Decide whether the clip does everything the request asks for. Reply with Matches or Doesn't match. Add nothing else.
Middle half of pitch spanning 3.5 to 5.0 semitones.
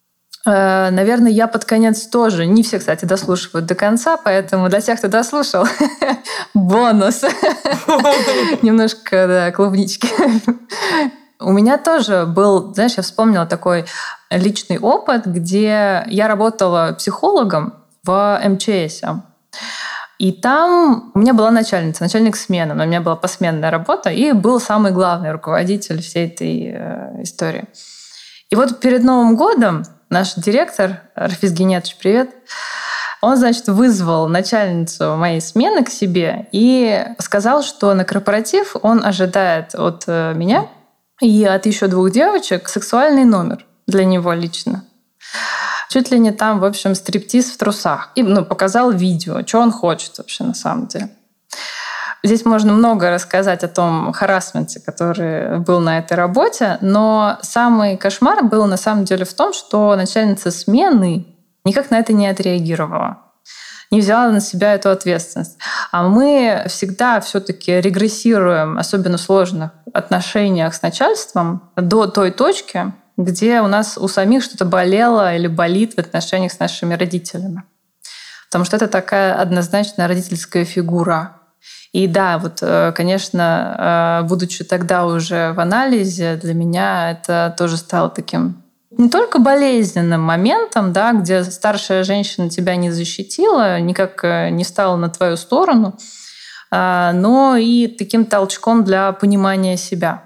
Matches